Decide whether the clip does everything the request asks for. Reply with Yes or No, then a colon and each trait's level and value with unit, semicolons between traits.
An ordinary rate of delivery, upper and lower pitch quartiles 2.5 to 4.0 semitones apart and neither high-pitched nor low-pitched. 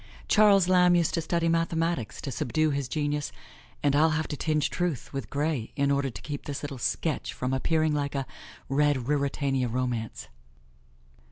Yes: average, 170 wpm; average, 3.0 semitones; medium, 145 Hz